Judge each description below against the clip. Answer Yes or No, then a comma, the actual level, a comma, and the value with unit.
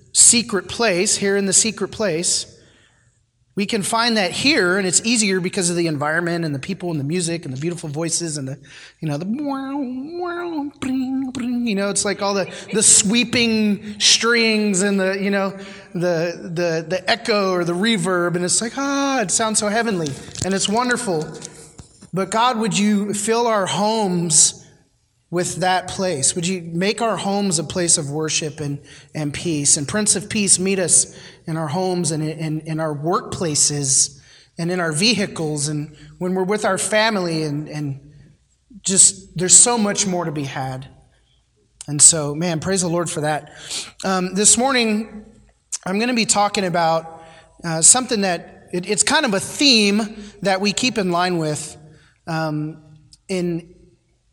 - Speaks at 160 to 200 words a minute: Yes, average, 170 wpm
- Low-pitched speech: No, medium, 185 Hz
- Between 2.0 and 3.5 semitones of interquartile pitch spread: No, average, 4.8 semitones